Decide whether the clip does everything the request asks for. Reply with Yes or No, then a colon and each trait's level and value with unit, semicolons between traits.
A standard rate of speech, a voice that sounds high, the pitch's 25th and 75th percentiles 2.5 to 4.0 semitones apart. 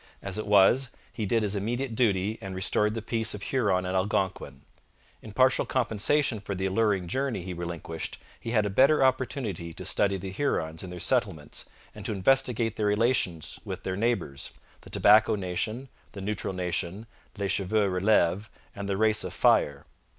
No: average, 175 wpm; low, 105 Hz; average, 3.4 semitones